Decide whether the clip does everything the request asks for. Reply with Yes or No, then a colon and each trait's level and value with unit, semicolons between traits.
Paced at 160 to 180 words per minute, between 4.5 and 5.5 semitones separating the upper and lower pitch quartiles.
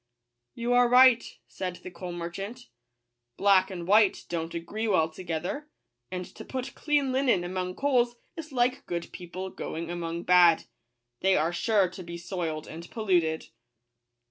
Yes: average, 165 wpm; average, 5.2 semitones